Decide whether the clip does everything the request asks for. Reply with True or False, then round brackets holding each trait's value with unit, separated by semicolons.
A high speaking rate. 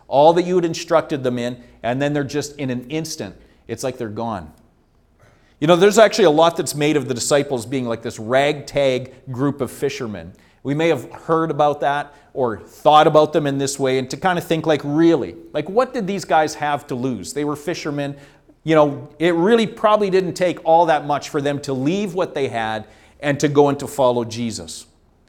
True (215 wpm)